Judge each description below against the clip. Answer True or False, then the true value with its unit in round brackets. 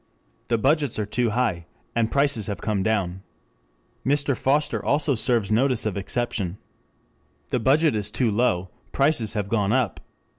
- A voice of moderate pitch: False (115 Hz)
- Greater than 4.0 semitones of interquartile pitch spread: True (4.5 semitones)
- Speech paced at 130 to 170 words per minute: True (150 wpm)